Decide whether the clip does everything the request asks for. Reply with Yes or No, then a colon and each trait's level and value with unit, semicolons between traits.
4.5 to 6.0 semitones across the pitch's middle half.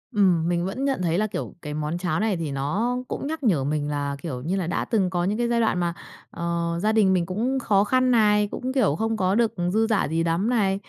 Yes: average, 4.9 semitones